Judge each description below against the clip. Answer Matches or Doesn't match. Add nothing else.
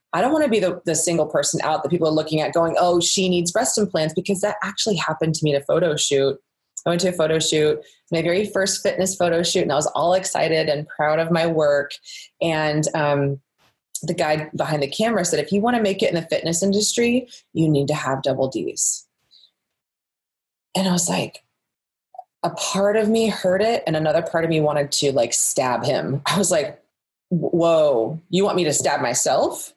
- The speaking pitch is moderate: Matches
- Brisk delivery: Matches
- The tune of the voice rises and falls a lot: Doesn't match